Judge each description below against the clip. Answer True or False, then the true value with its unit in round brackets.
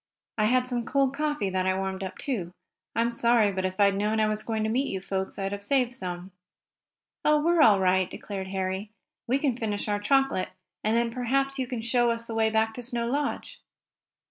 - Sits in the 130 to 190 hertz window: False (220 Hz)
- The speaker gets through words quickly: True (220 wpm)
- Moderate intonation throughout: True (4.4 semitones)